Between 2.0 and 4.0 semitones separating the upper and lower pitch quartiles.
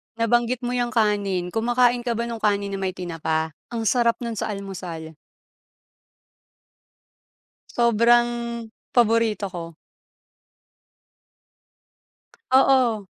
Yes: average, 3.7 semitones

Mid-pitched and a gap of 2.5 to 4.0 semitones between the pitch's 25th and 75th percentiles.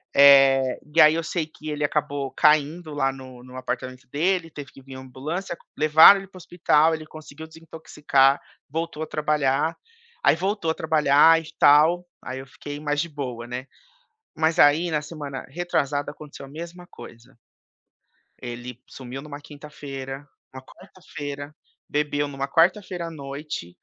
Yes: medium, 150 Hz; average, 2.9 semitones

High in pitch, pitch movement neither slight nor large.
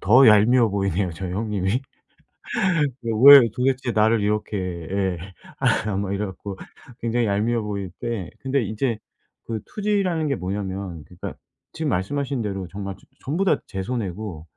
No: low, 105 Hz; average, 4.3 semitones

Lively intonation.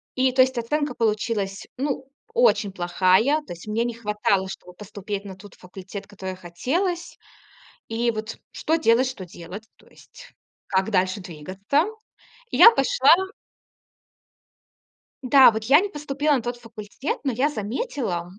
Yes: wide, 5.7 semitones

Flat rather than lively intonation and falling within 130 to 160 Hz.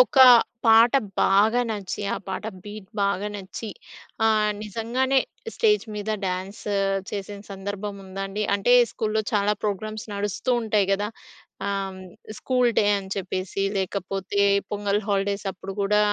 No: narrow, 1.8 semitones; high, 205 Hz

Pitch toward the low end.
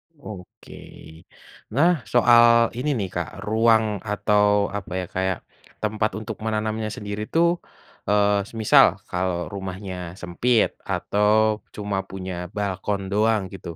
Yes: low, 105 Hz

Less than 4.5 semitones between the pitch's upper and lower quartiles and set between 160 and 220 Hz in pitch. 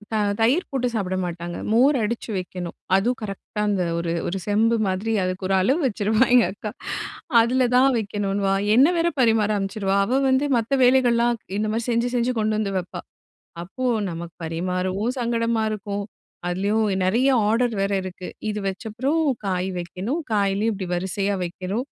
Yes: average, 3.9 semitones; high, 210 Hz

